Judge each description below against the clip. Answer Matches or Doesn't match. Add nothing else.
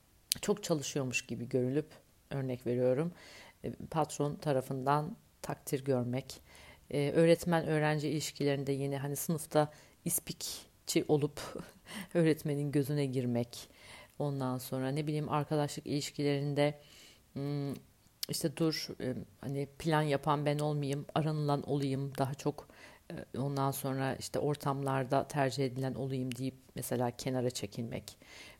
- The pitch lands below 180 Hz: Matches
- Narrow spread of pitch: Matches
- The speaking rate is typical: Matches